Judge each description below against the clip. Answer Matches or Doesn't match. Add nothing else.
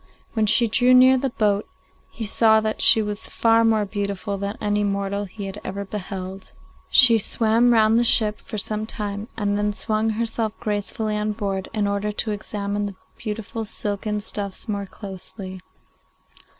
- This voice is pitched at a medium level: Doesn't match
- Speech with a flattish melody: Matches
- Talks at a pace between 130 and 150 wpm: Doesn't match